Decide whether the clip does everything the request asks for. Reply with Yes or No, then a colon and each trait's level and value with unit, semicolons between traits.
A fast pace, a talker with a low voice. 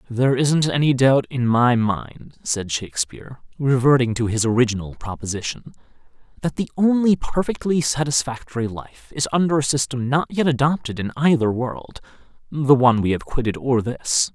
No: average, 150 wpm; low, 130 Hz